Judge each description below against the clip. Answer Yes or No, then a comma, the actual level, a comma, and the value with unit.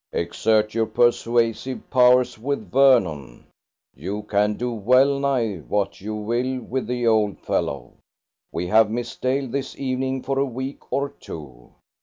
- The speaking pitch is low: Yes, low, 115 Hz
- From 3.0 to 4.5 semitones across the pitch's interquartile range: Yes, average, 3.9 semitones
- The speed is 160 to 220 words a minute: No, average, 145 wpm